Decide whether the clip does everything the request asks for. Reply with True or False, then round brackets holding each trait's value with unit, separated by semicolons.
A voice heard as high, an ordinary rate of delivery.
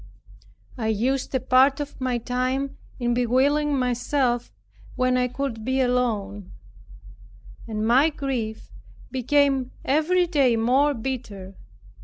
False (255 Hz; 115 wpm)